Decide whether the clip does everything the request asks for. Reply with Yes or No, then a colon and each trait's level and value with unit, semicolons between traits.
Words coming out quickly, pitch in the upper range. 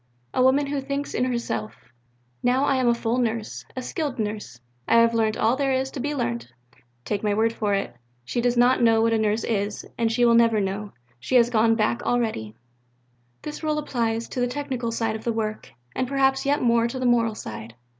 Yes: fast, 220 wpm; high, 235 Hz